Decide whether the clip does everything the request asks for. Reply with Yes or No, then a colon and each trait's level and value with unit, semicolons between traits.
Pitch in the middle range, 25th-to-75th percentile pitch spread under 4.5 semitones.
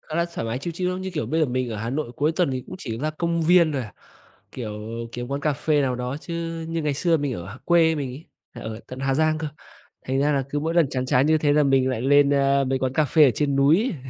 Yes: medium, 145 Hz; average, 3.7 semitones